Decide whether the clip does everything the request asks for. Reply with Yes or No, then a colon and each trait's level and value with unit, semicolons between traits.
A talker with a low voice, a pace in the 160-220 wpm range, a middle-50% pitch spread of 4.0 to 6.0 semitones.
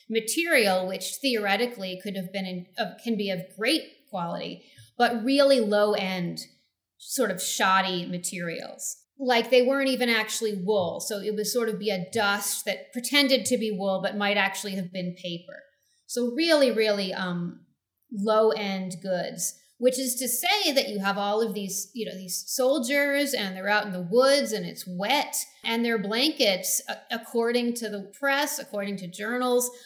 No: high, 215 Hz; average, 170 wpm; average, 4.5 semitones